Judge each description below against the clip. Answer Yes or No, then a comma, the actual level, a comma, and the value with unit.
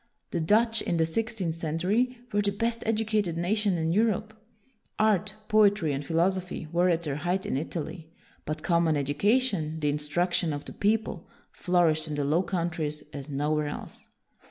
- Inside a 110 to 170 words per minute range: Yes, average, 160 wpm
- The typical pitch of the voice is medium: Yes, medium, 175 Hz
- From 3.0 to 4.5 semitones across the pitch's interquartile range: No, average, 4.9 semitones